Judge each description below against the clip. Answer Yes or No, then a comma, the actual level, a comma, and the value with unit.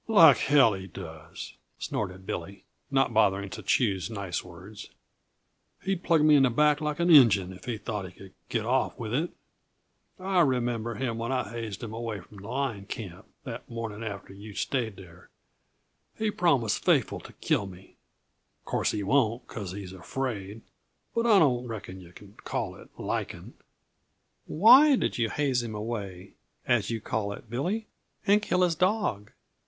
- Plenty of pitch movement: Yes, wide, 6.0 semitones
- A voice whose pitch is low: Yes, low, 115 Hz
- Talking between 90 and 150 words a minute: No, average, 170 wpm